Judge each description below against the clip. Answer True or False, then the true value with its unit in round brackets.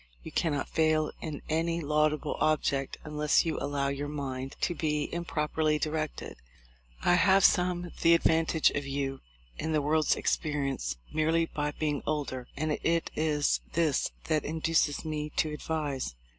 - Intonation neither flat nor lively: False (1.9 semitones)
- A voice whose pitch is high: False (155 Hz)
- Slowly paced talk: False (145 wpm)